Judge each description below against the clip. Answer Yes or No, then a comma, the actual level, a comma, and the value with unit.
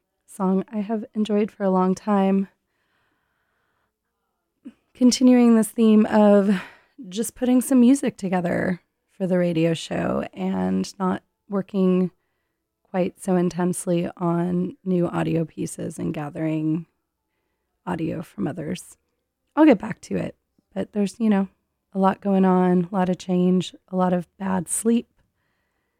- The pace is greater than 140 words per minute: No, slow, 135 wpm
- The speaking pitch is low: No, high, 190 Hz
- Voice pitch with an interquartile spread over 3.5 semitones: No, average, 3.2 semitones